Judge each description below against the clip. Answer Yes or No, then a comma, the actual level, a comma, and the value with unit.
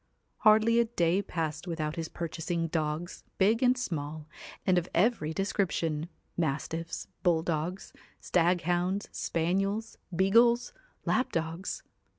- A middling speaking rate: No, slow, 115 wpm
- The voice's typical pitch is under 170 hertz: No, medium, 175 Hz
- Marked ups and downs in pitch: No, average, 3.7 semitones